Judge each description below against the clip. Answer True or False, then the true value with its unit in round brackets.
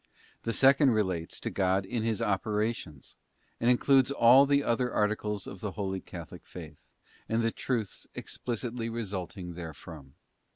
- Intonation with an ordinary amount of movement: True (4.0 semitones)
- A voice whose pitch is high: False (110 Hz)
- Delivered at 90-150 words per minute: True (140 wpm)